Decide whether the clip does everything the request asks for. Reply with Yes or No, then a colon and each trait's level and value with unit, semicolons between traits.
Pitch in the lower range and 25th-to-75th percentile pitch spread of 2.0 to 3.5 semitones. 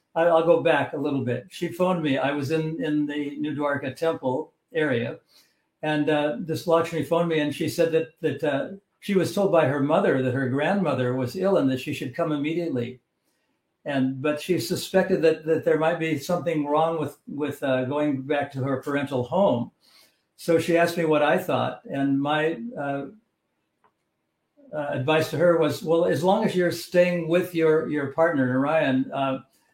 No: medium, 155 Hz; average, 3.0 semitones